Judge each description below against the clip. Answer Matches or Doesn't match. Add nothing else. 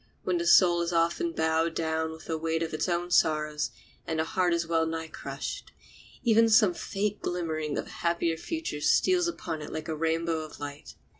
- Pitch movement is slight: Matches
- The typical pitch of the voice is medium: Matches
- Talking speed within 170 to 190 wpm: Doesn't match